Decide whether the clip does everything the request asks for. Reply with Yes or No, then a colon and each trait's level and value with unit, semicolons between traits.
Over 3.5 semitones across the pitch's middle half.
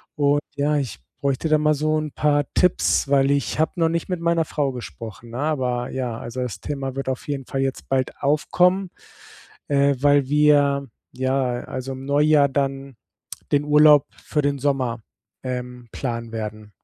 No: narrow, 2.4 semitones